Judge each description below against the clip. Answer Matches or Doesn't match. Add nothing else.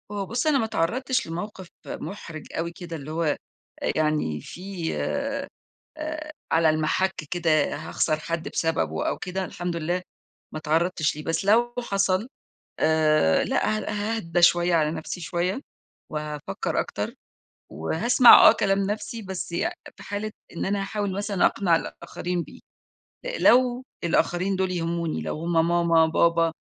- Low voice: Doesn't match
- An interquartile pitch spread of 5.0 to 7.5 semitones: Doesn't match